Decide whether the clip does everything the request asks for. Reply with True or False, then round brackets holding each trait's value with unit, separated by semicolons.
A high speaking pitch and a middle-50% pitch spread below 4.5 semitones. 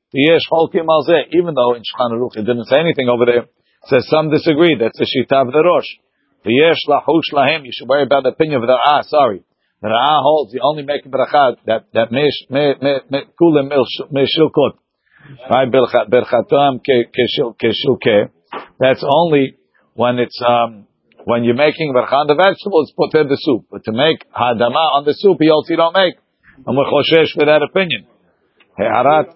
False (140 Hz; 4.1 semitones)